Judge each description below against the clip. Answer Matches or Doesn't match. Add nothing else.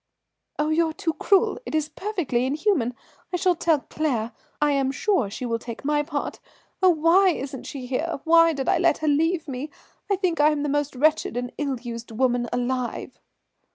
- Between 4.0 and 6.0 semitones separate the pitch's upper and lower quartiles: Matches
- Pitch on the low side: Doesn't match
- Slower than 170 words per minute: Doesn't match